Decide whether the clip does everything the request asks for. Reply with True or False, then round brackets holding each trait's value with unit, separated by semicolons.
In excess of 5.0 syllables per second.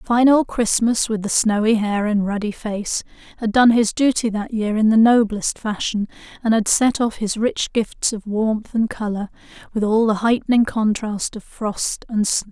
False (4.4 syllables/s)